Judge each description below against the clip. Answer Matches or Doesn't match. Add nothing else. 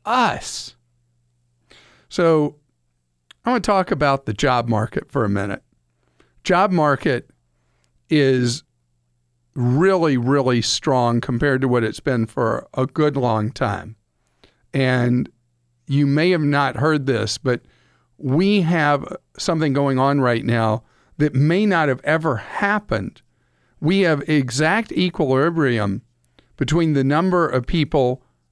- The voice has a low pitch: Matches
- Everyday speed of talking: Doesn't match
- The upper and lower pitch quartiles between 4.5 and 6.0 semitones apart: Matches